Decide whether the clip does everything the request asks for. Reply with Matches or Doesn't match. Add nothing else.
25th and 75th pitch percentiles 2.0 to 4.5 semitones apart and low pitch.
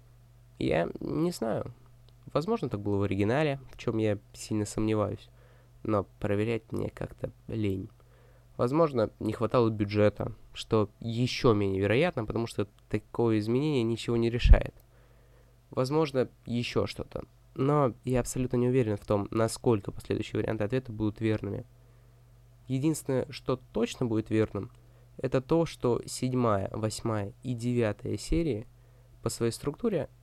Matches